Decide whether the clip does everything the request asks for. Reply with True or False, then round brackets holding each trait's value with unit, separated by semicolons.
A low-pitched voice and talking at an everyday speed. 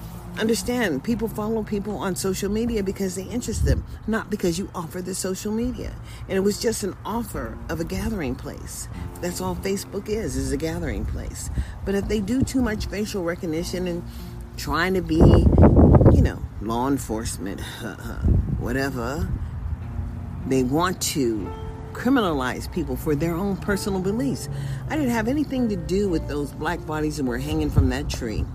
False (165 Hz; 165 wpm)